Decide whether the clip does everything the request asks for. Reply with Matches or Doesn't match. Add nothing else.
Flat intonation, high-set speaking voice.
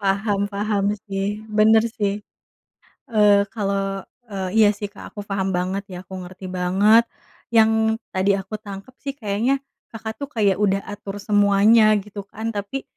Matches